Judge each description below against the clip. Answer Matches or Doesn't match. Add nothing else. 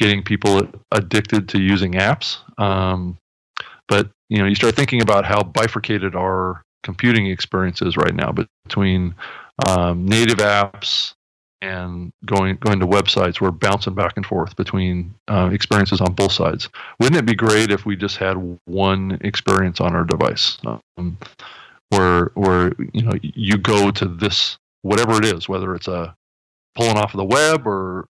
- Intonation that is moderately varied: Doesn't match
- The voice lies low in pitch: Matches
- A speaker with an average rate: Matches